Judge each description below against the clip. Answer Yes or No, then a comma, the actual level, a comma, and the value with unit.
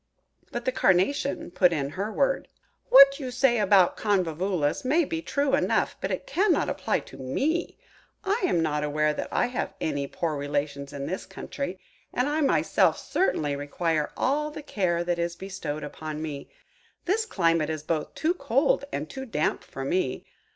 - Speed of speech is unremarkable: Yes, average, 175 wpm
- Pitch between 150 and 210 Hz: Yes, medium, 185 Hz